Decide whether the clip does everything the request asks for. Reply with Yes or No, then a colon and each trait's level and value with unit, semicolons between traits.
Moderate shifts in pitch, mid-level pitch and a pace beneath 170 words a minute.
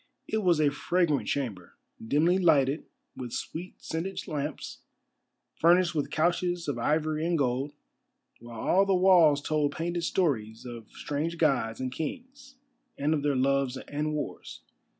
Yes: average, 4.0 semitones; medium, 150 Hz; average, 145 wpm